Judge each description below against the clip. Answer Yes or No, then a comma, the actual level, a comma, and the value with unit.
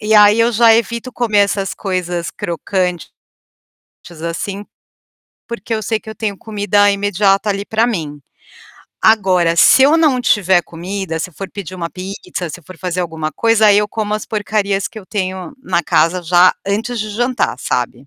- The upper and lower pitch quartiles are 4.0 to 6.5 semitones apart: No, average, 3.3 semitones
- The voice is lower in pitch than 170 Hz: No, high, 200 Hz